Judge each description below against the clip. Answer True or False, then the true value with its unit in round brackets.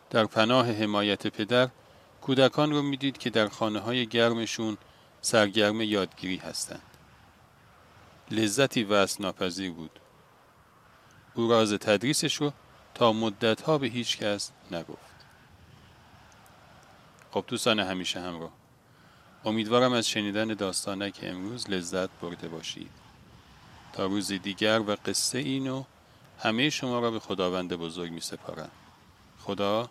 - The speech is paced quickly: False (110 wpm)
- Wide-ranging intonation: False (4.0 semitones)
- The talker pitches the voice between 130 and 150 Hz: False (110 Hz)